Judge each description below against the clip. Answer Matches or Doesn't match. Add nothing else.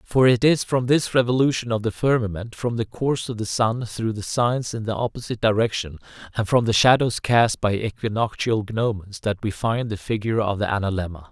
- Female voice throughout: Doesn't match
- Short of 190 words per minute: Doesn't match